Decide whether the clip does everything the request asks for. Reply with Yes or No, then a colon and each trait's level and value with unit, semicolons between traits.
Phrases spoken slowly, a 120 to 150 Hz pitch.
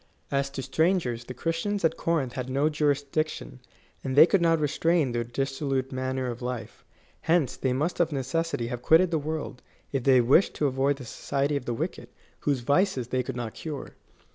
No: average, 190 wpm; medium, 140 Hz